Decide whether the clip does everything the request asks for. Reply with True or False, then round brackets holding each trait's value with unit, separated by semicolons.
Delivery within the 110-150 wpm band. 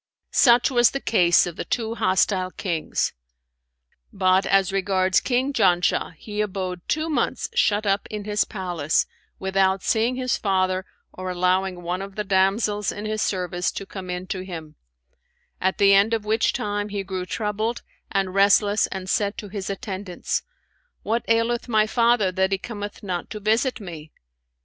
False (165 wpm)